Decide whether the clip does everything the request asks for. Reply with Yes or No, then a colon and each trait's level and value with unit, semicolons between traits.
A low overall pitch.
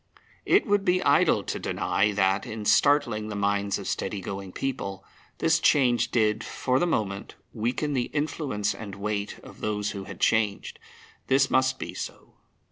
Yes: low, 110 Hz